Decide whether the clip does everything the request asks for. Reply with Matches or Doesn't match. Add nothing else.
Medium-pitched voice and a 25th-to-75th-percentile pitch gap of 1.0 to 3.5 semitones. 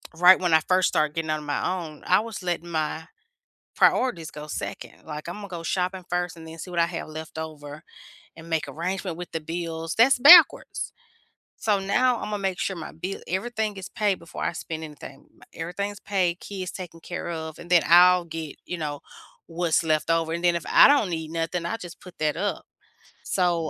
Matches